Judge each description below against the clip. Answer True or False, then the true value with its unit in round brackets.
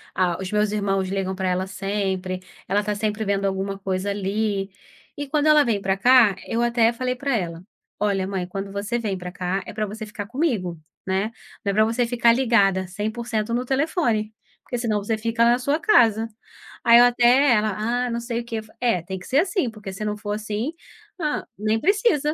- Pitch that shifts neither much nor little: True (3.5 semitones)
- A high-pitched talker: True (215 Hz)